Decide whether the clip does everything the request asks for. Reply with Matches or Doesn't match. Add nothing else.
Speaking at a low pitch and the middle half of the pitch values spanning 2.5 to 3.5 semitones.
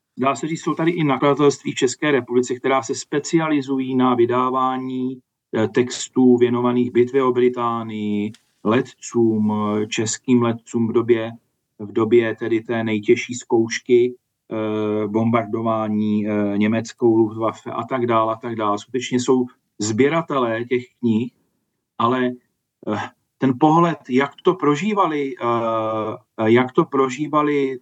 Matches